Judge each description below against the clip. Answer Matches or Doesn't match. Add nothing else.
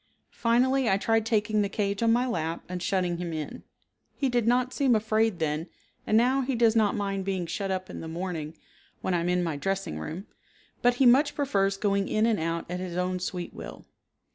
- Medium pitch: Doesn't match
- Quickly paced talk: Matches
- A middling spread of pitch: Matches